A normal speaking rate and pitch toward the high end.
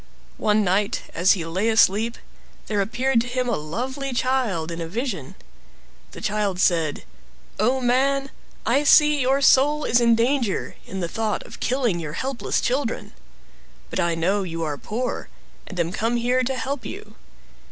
Yes: average, 165 wpm; high, 230 Hz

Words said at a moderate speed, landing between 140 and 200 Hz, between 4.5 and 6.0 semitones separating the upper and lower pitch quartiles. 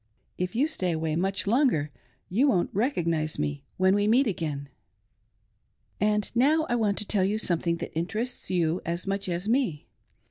Yes: average, 170 wpm; high, 190 Hz; average, 4.9 semitones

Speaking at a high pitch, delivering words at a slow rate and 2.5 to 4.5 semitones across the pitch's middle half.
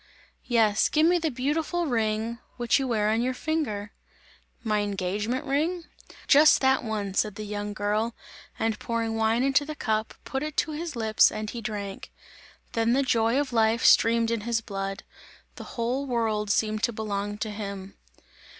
No: high, 225 Hz; average, 170 wpm; average, 3.8 semitones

